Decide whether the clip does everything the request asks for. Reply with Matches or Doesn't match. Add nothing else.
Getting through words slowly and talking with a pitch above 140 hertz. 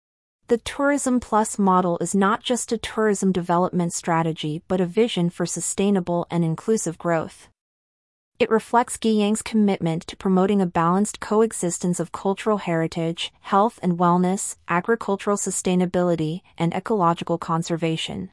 Matches